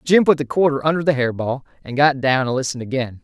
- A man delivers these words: Yes, male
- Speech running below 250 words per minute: No, fast, 260 wpm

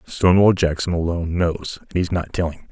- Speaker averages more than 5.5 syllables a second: Yes, 5.7 syllables/s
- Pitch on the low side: Yes, very low, 85 Hz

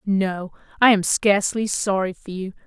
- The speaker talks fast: No, average, 160 wpm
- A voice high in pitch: Yes, high, 195 Hz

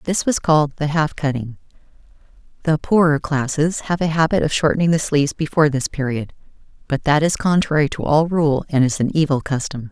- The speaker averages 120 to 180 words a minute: No, average, 190 wpm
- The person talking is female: Yes, female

